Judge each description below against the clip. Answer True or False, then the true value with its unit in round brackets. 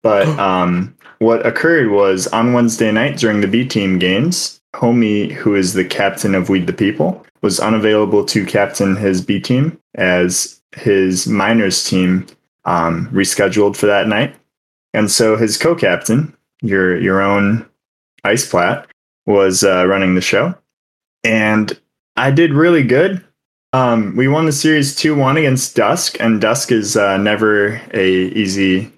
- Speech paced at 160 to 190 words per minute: False (150 wpm)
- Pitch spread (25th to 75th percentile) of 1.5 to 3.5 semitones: False (4.0 semitones)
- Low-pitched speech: True (105 Hz)